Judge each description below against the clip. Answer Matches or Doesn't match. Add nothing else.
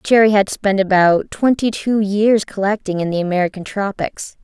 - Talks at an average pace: Matches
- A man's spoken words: Doesn't match